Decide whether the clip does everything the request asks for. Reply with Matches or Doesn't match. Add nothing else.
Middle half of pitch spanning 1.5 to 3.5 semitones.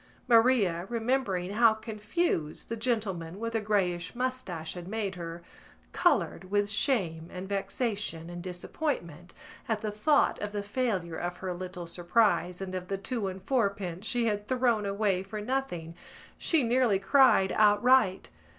Doesn't match